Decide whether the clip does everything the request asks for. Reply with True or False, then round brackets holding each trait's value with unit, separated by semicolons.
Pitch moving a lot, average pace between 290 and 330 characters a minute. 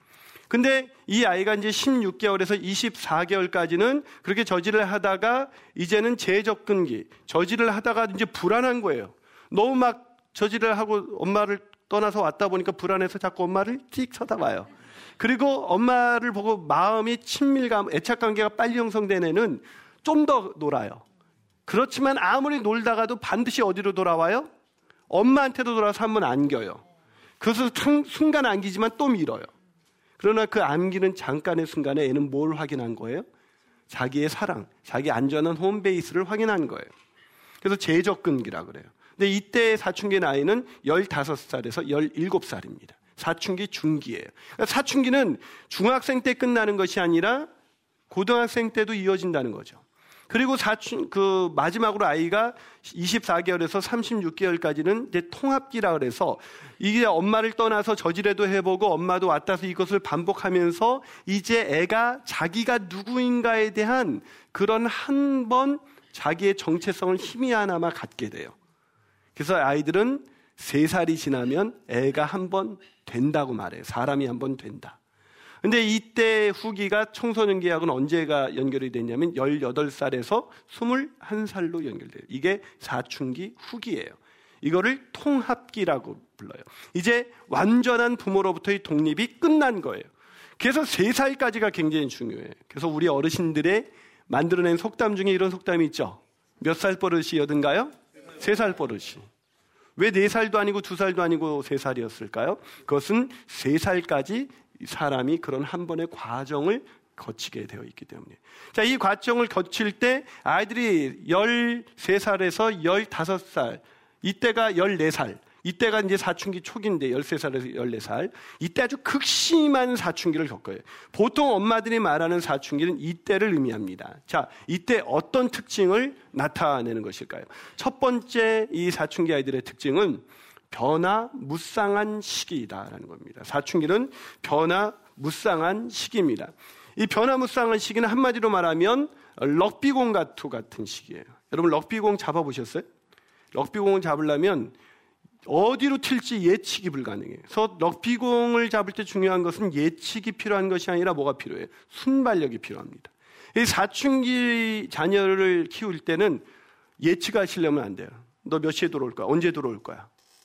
True (5.7 semitones; 310 characters per minute)